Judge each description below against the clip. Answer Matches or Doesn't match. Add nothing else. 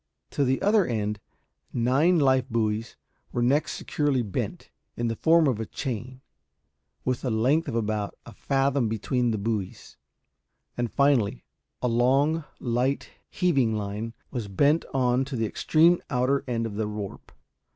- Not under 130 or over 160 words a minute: Matches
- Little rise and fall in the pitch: Doesn't match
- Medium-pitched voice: Doesn't match